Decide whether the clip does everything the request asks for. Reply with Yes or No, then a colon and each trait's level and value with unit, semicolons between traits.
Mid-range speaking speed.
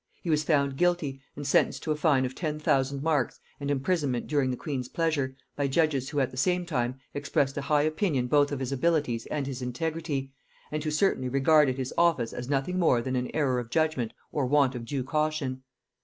No: fast, 210 wpm